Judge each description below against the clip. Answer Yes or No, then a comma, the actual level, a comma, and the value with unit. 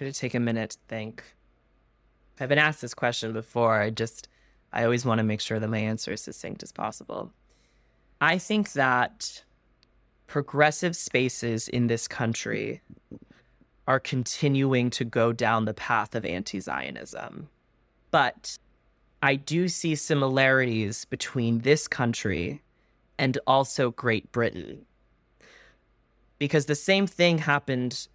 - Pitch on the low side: Yes, low, 125 Hz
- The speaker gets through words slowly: Yes, slow, 130 wpm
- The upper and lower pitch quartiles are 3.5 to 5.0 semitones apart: Yes, average, 4.1 semitones